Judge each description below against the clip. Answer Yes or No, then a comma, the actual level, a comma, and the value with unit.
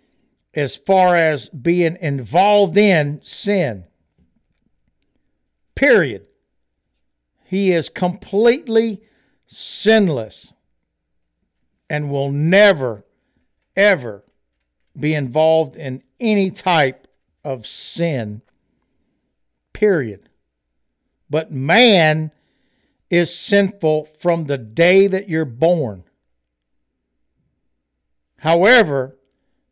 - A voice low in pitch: No, medium, 150 Hz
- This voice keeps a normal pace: No, slow, 70 wpm